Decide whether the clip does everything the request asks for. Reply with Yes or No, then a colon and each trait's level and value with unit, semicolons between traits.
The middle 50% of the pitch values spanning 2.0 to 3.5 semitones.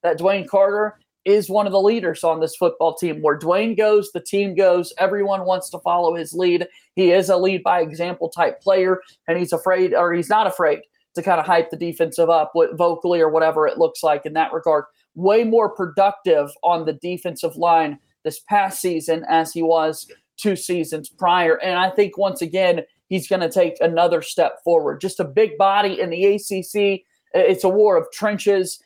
Yes: average, 3.1 semitones